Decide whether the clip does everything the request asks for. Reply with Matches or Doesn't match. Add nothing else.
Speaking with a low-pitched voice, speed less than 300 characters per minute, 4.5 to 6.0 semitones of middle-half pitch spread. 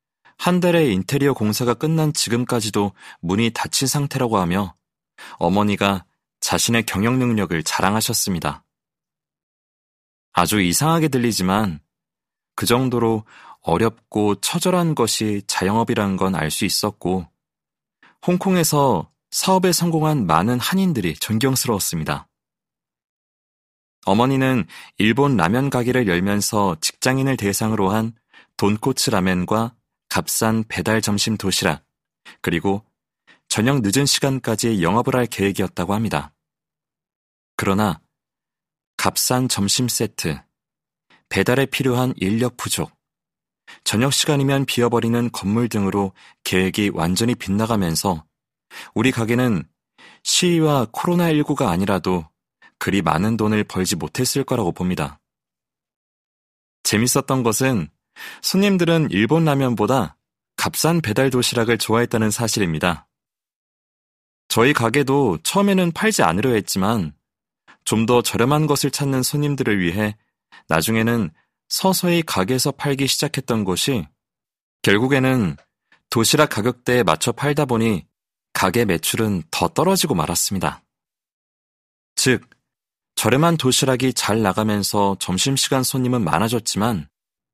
Matches